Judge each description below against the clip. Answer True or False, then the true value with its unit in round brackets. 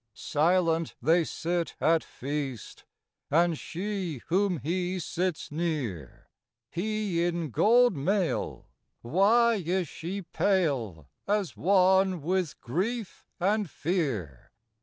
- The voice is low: False (175 Hz)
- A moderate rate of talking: False (100 wpm)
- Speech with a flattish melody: False (3.9 semitones)